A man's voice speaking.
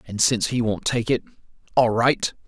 Yes: male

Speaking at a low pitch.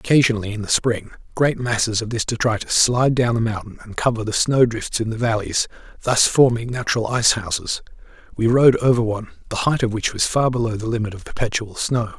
Yes: low, 115 Hz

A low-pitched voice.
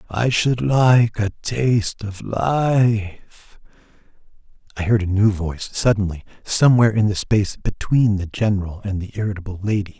Yes: low, 105 Hz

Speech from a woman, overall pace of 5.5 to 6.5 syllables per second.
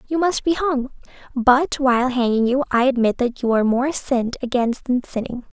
No: female; 5.3 syllables/s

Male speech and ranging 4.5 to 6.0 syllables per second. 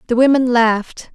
No: female; 5.5 syllables/s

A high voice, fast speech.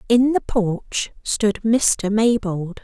No: high, 215 Hz; slow, 125 wpm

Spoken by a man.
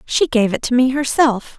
No: female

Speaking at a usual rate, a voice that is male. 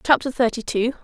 No: average, 175 wpm; female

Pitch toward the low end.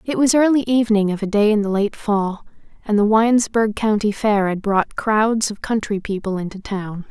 No: high, 210 Hz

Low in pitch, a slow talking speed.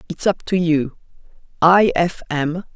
No: medium, 170 Hz; slow, 130 wpm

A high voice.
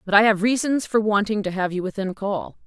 Yes: high, 205 Hz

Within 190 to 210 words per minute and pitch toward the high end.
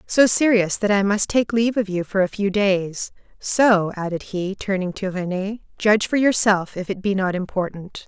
Yes: average, 200 wpm; high, 200 Hz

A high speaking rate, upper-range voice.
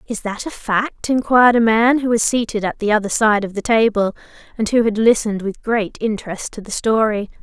Yes: fast, 220 wpm; high, 220 Hz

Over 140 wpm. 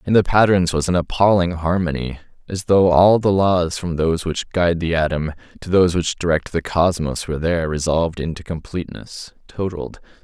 Yes: average, 165 wpm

